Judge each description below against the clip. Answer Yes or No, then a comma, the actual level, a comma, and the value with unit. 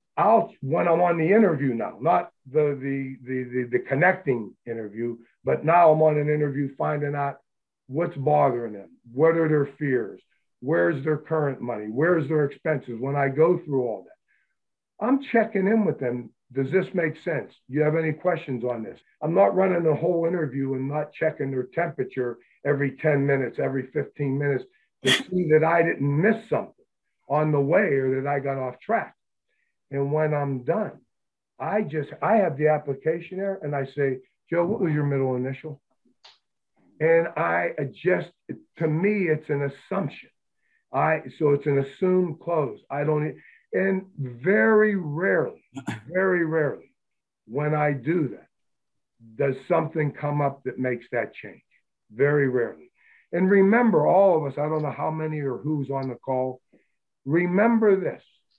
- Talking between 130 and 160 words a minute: No, average, 170 wpm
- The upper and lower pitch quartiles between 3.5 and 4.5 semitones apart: Yes, average, 3.8 semitones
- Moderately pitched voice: Yes, medium, 150 Hz